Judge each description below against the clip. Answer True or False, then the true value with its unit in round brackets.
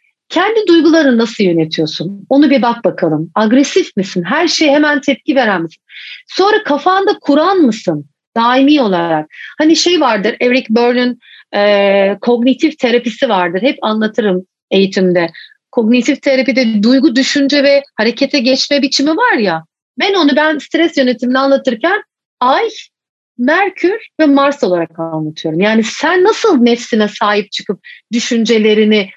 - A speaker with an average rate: False (130 wpm)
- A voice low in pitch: False (255 Hz)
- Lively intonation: True (6.2 semitones)